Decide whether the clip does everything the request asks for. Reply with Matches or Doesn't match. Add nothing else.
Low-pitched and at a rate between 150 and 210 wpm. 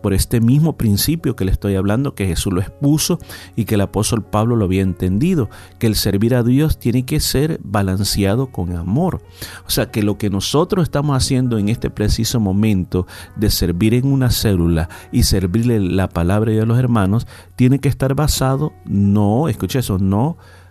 Matches